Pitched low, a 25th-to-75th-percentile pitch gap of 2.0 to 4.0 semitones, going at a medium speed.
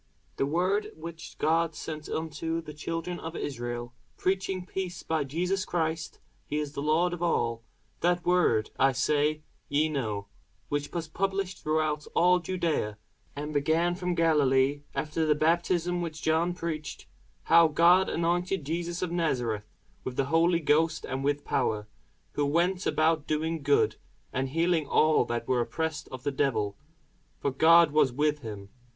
No: medium, 160 Hz; average, 3.1 semitones; average, 155 wpm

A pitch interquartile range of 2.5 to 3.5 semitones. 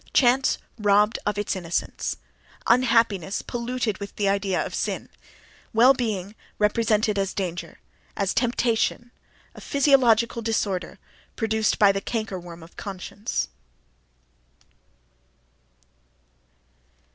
Yes: average, 3.0 semitones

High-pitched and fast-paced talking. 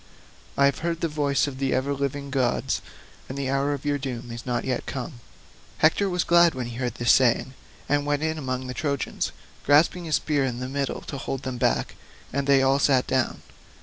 No: low, 135 Hz; fast, 215 wpm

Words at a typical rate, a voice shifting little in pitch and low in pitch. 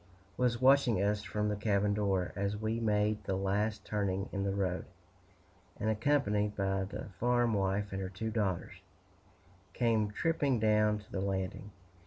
Yes: average, 165 wpm; narrow, 2.0 semitones; low, 105 Hz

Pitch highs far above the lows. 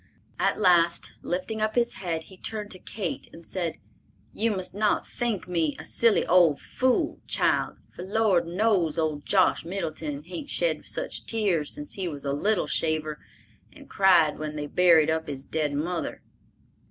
No: average, 4.7 semitones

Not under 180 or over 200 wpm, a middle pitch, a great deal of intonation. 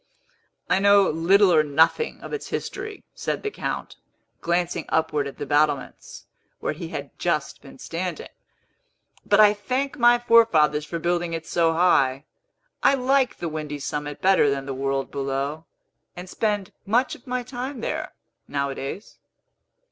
No: average, 150 wpm; medium, 170 Hz; wide, 6.8 semitones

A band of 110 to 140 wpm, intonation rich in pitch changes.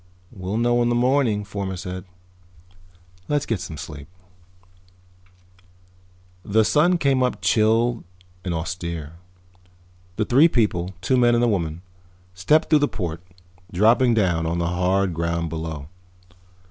Yes: slow, 135 wpm; wide, 5.9 semitones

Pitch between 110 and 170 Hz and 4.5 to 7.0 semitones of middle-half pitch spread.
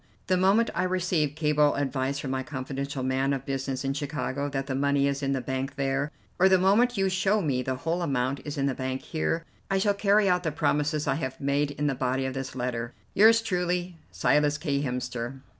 Yes: medium, 140 Hz; average, 4.9 semitones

